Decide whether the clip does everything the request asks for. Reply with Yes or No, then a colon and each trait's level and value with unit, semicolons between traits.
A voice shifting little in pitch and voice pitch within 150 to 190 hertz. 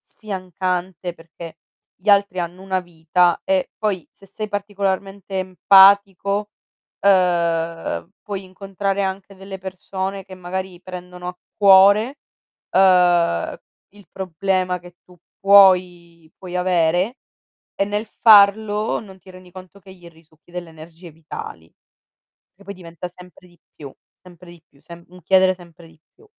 Yes: narrow, 2.2 semitones; medium, 185 Hz